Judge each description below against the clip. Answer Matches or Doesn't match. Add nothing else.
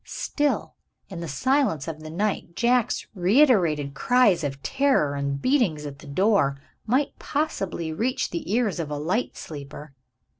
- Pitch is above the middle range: Doesn't match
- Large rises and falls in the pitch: Matches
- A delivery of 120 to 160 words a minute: Matches